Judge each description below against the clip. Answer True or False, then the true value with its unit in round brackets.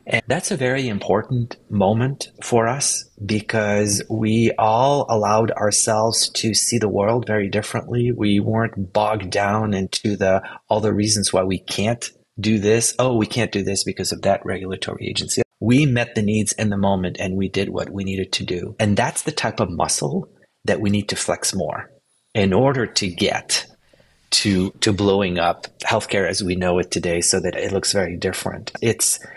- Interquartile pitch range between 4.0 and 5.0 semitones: False (2.7 semitones)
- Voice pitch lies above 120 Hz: False (105 Hz)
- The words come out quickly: False (185 wpm)